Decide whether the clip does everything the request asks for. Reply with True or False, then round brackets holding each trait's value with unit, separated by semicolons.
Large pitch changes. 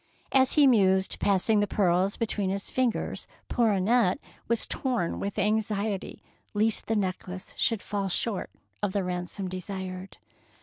False (2.8 semitones)